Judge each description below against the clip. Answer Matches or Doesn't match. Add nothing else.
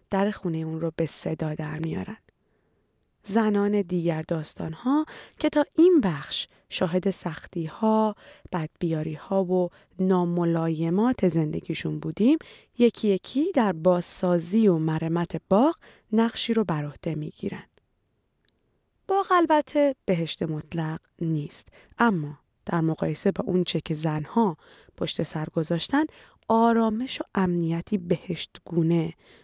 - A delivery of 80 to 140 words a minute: Matches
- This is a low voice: Doesn't match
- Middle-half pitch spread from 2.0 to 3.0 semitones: Doesn't match